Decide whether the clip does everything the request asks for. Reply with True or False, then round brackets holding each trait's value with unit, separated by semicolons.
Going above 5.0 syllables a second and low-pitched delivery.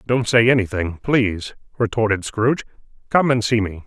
True (5.4 syllables/s; 110 Hz)